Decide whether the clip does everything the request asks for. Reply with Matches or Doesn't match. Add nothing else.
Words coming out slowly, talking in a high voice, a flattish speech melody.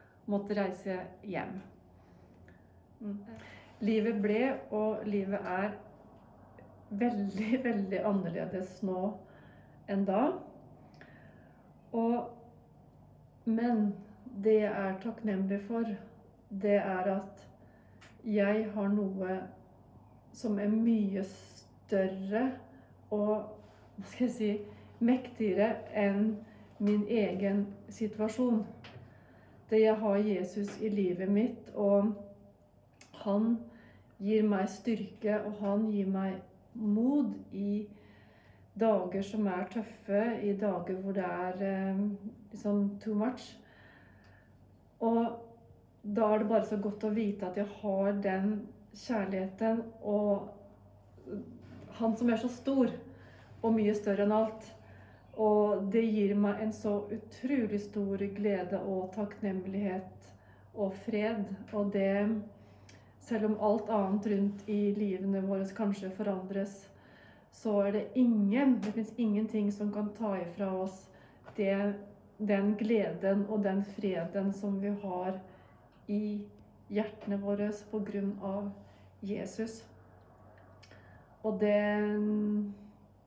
Matches